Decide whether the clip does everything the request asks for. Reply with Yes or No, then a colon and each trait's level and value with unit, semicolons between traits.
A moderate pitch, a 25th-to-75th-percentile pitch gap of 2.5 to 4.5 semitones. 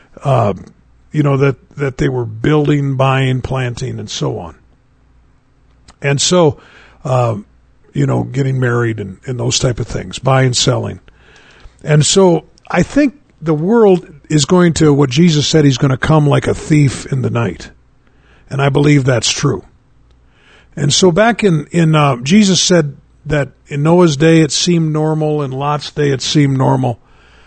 Yes: medium, 145 Hz; average, 3.7 semitones